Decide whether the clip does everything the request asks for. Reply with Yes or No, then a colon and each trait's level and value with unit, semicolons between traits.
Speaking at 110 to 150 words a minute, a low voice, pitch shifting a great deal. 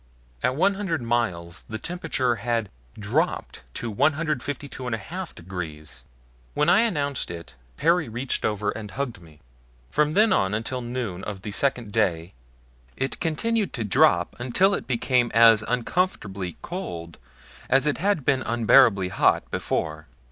Yes: average, 140 wpm; low, 120 Hz; wide, 7.0 semitones